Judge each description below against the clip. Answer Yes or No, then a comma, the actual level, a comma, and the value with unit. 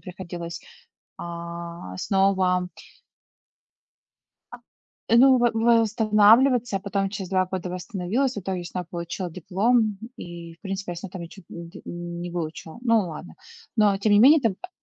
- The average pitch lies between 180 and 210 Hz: Yes, high, 190 Hz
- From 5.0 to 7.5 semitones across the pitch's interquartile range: No, average, 3.6 semitones